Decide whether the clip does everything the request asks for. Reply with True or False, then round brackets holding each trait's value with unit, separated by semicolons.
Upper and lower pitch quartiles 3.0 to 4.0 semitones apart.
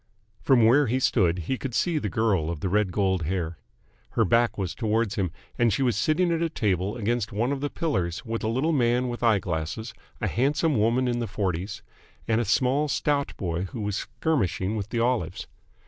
False (4.9 semitones)